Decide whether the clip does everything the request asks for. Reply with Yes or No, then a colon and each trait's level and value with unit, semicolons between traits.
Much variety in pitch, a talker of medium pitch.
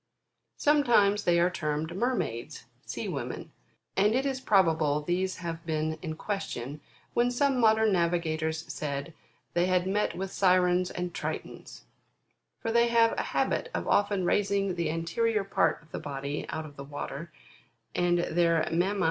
No: average, 4.5 semitones; medium, 175 Hz